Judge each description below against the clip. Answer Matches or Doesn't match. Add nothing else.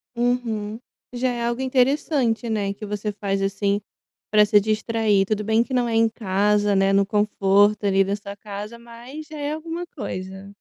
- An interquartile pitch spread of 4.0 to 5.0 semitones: Doesn't match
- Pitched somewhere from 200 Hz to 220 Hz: Matches